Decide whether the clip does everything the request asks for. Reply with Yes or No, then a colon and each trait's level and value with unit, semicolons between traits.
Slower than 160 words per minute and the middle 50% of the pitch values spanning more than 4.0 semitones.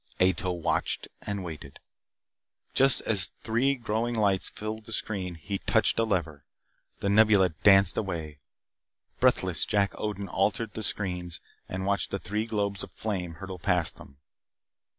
No: average, 150 wpm; average, 3.1 semitones